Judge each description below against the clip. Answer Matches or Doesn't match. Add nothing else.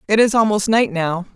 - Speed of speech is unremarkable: Doesn't match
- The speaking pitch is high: Matches